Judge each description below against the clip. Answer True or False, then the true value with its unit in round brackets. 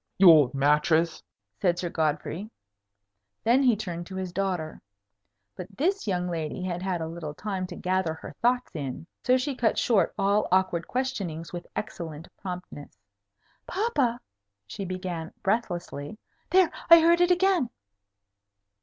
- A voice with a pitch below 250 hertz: True (185 Hz)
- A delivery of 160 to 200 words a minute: False (145 wpm)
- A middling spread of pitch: False (6.0 semitones)